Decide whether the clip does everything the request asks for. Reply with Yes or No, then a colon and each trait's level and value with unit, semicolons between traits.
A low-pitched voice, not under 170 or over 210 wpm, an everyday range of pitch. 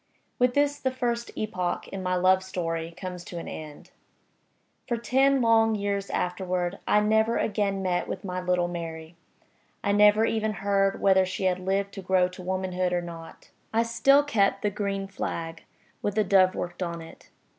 No: high, 195 Hz; average, 175 wpm; average, 3.1 semitones